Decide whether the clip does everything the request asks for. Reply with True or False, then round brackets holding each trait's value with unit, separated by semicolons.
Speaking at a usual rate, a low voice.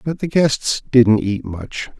True (180 wpm; 125 Hz)